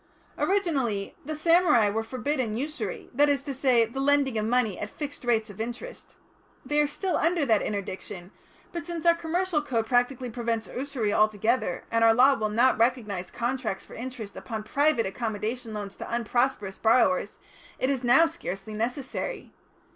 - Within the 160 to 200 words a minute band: Yes, average, 165 wpm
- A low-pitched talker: No, high, 245 Hz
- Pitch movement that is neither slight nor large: Yes, average, 4.7 semitones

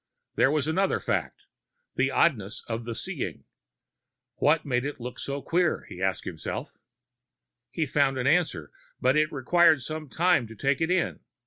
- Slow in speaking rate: No, average, 160 wpm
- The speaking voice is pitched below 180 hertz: Yes, medium, 140 Hz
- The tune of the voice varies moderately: Yes, average, 4.5 semitones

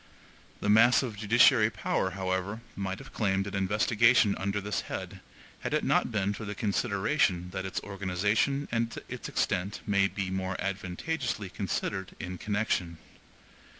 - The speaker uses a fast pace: No, average, 150 wpm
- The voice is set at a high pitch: No, low, 100 Hz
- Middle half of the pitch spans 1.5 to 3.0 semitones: Yes, narrow, 2.4 semitones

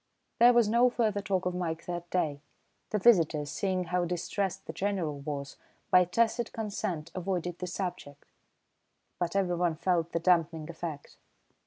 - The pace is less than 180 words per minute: Yes, average, 150 wpm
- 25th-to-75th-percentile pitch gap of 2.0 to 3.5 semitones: Yes, average, 3.1 semitones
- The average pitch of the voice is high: No, medium, 180 Hz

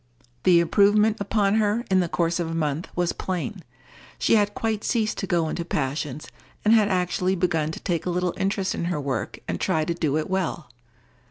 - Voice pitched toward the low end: No, medium, 180 Hz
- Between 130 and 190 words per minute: No, average, 200 wpm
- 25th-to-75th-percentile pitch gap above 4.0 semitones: No, average, 3.6 semitones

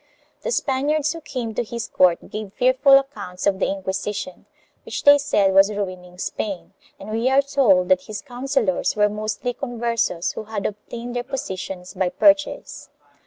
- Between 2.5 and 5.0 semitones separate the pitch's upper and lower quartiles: No, wide, 5.5 semitones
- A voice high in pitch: Yes, high, 215 Hz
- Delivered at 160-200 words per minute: Yes, average, 165 wpm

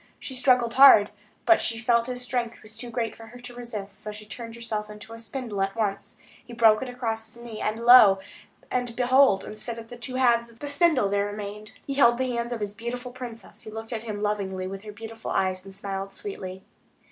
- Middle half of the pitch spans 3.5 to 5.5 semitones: No, average, 2.7 semitones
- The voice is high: Yes, high, 230 Hz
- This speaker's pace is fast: Yes, fast, 215 wpm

